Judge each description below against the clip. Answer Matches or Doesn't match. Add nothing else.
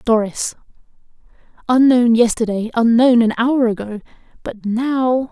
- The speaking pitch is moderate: Doesn't match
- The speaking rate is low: Matches